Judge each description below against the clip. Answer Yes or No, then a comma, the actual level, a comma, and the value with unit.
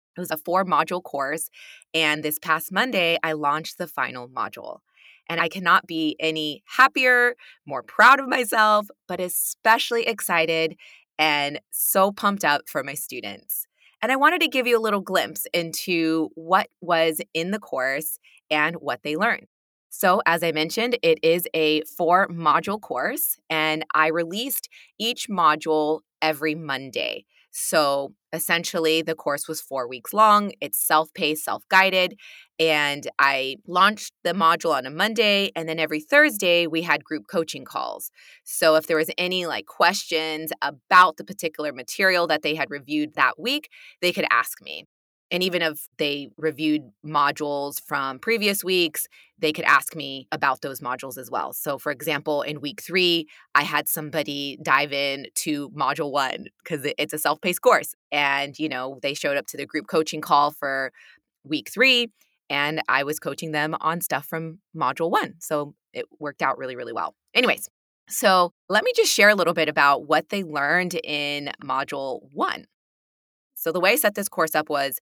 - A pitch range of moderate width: Yes, average, 3.7 semitones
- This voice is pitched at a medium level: Yes, medium, 160 Hz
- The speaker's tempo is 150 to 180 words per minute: Yes, average, 170 wpm